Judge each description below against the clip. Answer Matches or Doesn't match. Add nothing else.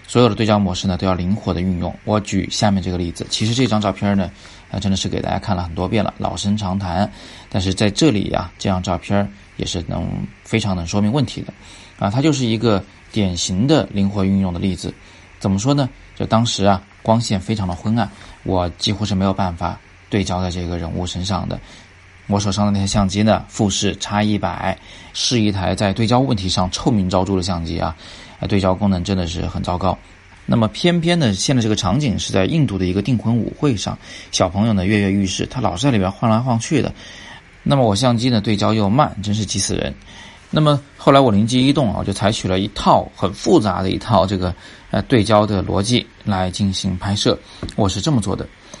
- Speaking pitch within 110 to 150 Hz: Doesn't match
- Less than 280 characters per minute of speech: Doesn't match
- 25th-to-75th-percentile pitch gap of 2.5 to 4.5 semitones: Matches